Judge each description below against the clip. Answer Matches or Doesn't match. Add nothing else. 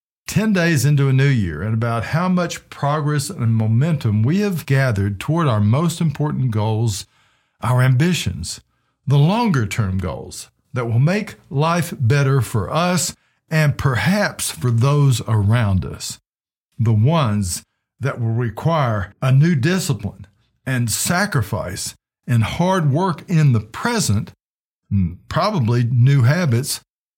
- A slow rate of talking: Matches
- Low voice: Matches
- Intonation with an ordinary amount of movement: Doesn't match